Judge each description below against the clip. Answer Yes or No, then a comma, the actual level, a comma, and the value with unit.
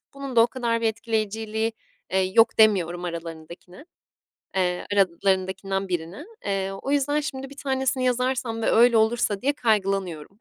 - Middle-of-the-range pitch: No, high, 220 Hz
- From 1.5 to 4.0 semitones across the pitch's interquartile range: No, average, 4.7 semitones